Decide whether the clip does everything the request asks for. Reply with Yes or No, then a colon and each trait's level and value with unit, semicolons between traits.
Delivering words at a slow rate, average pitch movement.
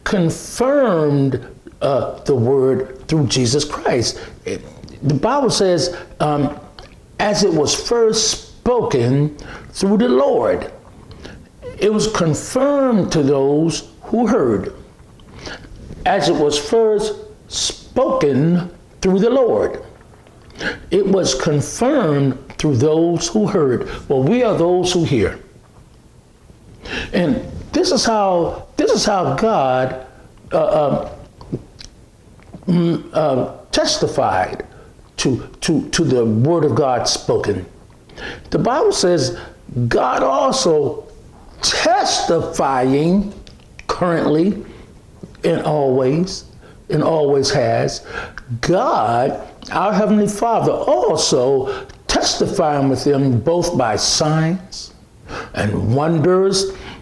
No: slow, 95 wpm; wide, 7.2 semitones